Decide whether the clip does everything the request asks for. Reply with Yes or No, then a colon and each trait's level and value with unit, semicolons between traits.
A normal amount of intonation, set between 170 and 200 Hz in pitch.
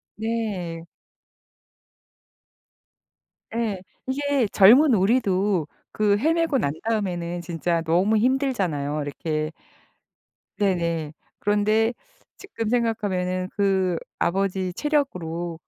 Yes: average, 4.8 semitones; high, 195 Hz